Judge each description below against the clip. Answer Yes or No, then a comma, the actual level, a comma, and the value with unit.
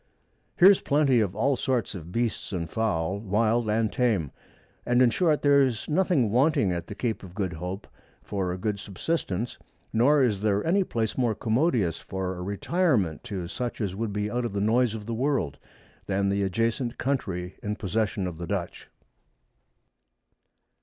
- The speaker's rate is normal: Yes, average, 170 wpm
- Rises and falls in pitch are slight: No, average, 4.5 semitones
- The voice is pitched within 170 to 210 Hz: No, low, 110 Hz